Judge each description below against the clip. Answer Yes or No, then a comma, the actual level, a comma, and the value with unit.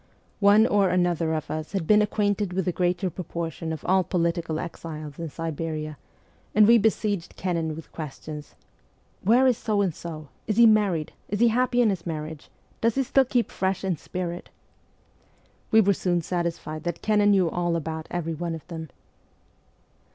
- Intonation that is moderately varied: Yes, average, 4.2 semitones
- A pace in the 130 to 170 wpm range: No, average, 180 wpm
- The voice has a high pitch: No, medium, 175 Hz